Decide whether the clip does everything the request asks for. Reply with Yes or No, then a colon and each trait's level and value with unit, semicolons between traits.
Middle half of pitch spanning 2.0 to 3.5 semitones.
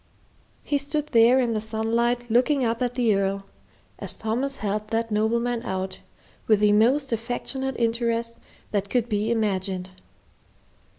Yes: narrow, 2.5 semitones